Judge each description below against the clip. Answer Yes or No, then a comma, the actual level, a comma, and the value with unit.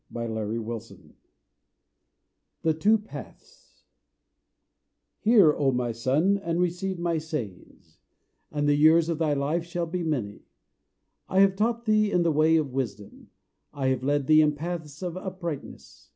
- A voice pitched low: No, medium, 155 Hz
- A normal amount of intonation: Yes, average, 4.8 semitones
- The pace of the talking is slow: No, average, 145 wpm